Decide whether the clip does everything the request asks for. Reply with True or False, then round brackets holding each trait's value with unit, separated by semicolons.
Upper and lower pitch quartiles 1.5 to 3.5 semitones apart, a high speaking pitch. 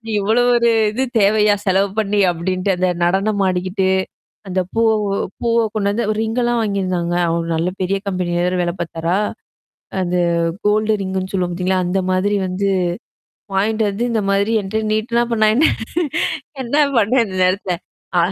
True (3.0 semitones; 195 Hz)